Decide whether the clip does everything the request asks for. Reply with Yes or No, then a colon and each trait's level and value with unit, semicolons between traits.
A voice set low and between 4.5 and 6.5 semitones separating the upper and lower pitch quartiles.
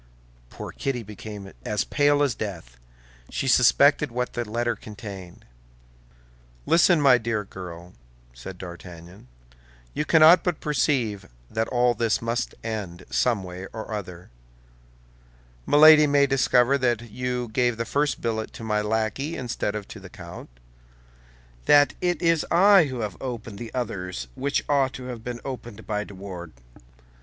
Yes: low, 115 Hz; average, 5.0 semitones